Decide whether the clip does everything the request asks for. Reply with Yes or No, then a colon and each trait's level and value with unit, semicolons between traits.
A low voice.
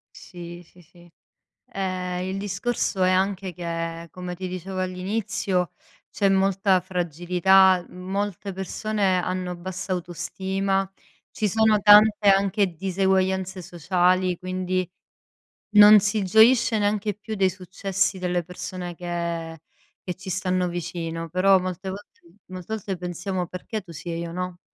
No: medium, 185 Hz